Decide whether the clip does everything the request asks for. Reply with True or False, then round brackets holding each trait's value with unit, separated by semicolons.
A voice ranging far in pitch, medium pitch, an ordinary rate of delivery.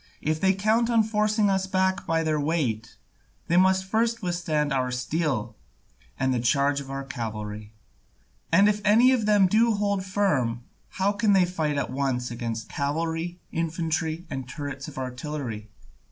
True (6.5 semitones; 160 Hz; 160 wpm)